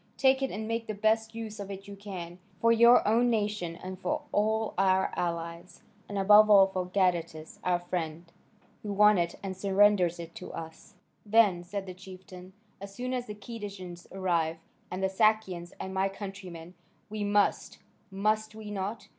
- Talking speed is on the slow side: No, average, 175 wpm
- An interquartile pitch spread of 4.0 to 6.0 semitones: No, average, 3.0 semitones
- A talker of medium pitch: No, high, 195 Hz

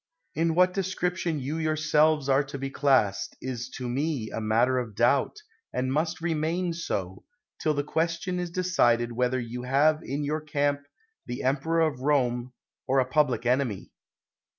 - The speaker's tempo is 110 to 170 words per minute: Yes, average, 160 wpm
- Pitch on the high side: No, medium, 140 Hz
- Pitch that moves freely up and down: No, average, 4.2 semitones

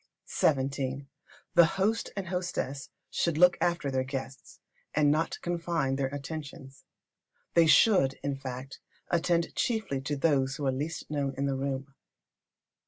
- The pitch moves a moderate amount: Yes, average, 3.9 semitones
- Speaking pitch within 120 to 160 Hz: Yes, medium, 140 Hz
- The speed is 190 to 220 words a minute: No, average, 145 wpm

